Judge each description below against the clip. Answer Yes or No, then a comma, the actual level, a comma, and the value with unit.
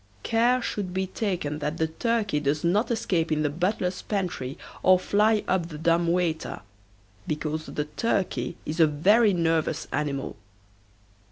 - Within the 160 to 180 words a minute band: No, average, 150 wpm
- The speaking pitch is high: No, medium, 170 Hz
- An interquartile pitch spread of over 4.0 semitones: Yes, average, 4.7 semitones